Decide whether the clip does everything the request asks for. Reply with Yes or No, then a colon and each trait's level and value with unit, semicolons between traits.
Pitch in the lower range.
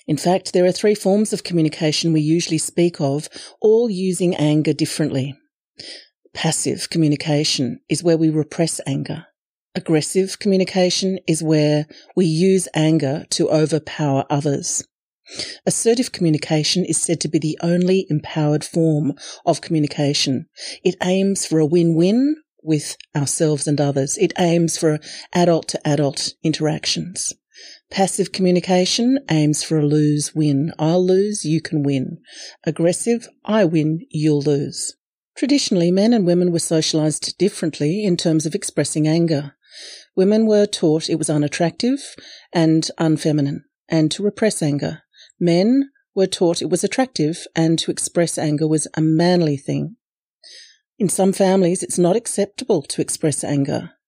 No: medium, 165 Hz